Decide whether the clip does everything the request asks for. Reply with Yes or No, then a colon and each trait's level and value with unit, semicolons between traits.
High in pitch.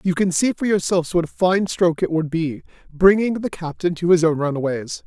No: medium, 175 Hz